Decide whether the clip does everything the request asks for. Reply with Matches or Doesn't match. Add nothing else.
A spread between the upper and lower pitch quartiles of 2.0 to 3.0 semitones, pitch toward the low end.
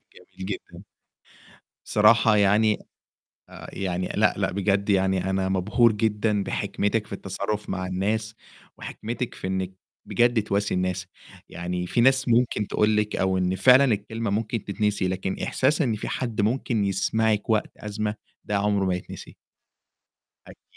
Matches